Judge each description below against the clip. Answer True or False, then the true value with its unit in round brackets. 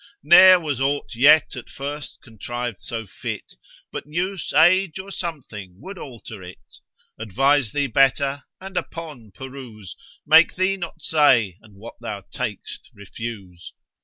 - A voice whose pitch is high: False (135 Hz)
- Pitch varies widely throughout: True (6.4 semitones)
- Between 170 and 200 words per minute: False (135 wpm)